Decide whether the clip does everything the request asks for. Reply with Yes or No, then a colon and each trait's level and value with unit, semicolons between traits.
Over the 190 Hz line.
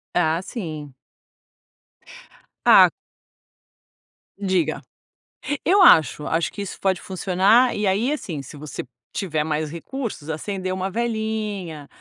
No: medium, 185 Hz